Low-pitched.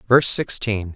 Yes: low, 110 Hz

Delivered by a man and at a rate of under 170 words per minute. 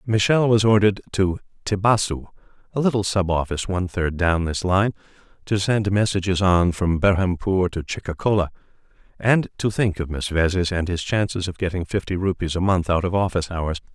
No: male; average, 175 wpm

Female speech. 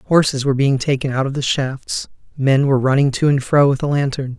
No: male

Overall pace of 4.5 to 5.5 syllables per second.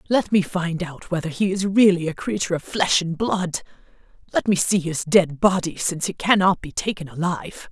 Yes: 5.3 syllables/s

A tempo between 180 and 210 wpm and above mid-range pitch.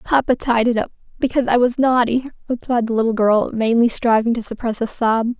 Yes: average, 200 wpm; high, 235 Hz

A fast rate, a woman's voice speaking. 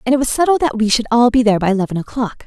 Yes: fast, 315 wpm; female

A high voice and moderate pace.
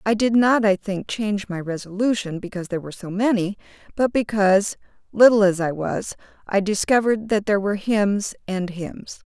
Yes: high, 205 Hz; average, 175 wpm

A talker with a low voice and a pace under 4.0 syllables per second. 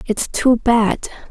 No: high, 230 Hz; 3.0 syllables/s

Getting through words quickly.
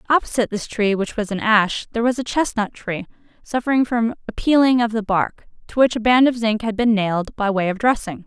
Yes: fast, 230 wpm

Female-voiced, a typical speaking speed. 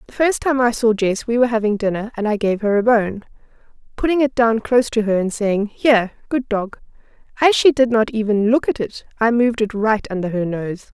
No: female; fast, 230 wpm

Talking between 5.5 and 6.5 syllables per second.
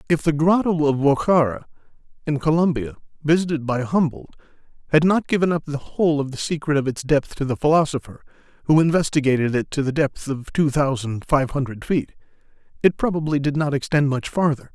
Yes: 5.7 syllables/s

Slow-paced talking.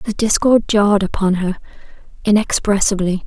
Yes: slow, 110 wpm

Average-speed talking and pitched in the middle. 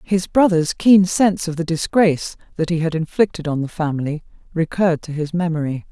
Yes: average, 185 wpm; medium, 170 Hz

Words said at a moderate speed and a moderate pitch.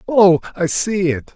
Yes: average, 180 wpm; medium, 180 Hz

